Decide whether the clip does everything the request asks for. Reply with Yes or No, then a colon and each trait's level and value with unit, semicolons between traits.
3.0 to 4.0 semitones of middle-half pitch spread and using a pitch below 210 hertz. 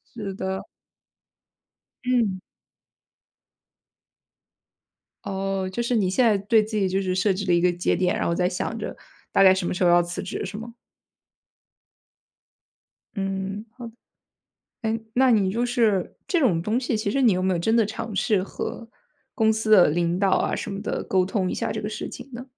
Yes: average, 3.3 semitones; high, 200 Hz